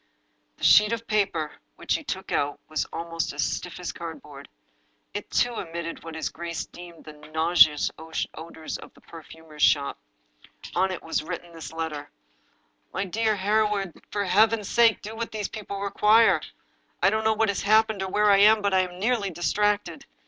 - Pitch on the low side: No, high, 190 Hz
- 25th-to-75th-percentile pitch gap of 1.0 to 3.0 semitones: No, average, 4.4 semitones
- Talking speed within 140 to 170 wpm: No, average, 180 wpm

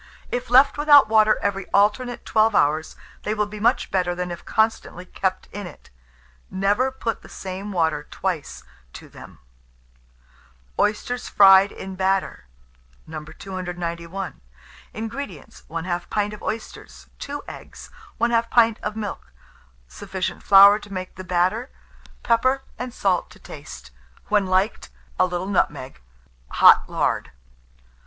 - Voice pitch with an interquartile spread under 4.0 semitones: Yes, average, 3.6 semitones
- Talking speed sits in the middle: No, slow, 130 wpm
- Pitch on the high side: Yes, high, 195 Hz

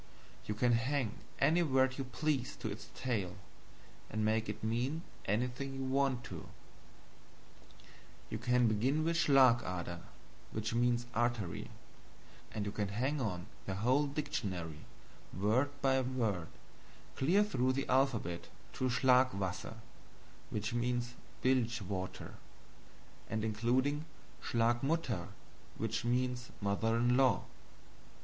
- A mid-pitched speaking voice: No, low, 120 Hz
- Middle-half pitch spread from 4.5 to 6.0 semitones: No, average, 3.7 semitones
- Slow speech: Yes, slow, 125 wpm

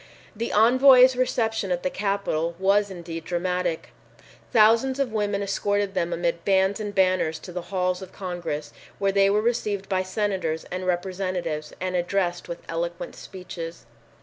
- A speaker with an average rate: Yes, average, 150 wpm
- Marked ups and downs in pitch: No, average, 2.7 semitones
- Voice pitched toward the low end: No, high, 190 Hz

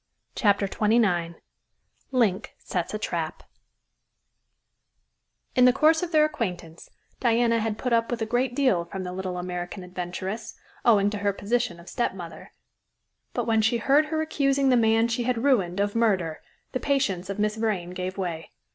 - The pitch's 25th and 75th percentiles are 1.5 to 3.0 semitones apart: No, average, 5.0 semitones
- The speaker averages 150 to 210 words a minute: Yes, average, 165 wpm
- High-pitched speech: Yes, high, 215 Hz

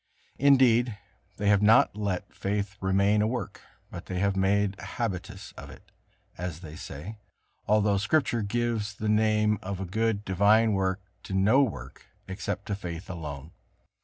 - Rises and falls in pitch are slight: Yes, narrow, 2.3 semitones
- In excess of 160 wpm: No, average, 155 wpm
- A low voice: Yes, low, 100 Hz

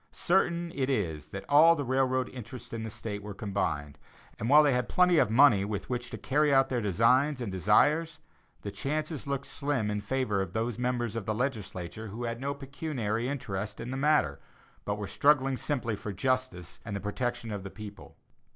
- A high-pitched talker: No, low, 120 Hz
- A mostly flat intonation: No, average, 5.0 semitones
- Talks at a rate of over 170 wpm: Yes, average, 195 wpm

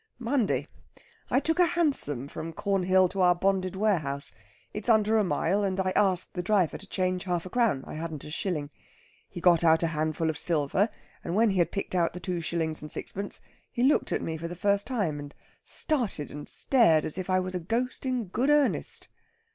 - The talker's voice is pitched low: No, medium, 185 Hz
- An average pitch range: Yes, average, 4.5 semitones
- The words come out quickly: Yes, fast, 210 wpm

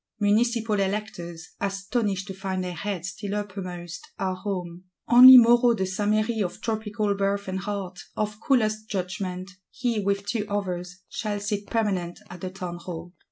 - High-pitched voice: Yes, high, 200 Hz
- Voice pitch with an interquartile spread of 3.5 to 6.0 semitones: No, narrow, 2.6 semitones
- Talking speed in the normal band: Yes, average, 155 wpm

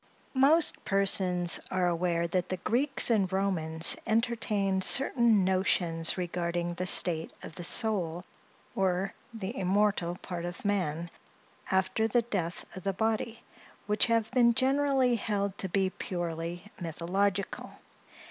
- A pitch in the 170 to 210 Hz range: Yes, high, 190 Hz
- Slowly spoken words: Yes, slow, 130 wpm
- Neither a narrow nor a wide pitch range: Yes, average, 4.0 semitones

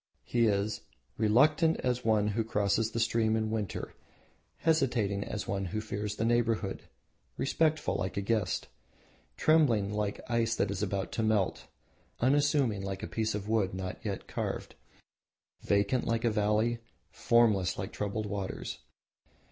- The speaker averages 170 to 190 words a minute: No, average, 145 wpm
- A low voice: Yes, low, 110 Hz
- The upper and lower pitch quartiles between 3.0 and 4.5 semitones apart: No, narrow, 2.6 semitones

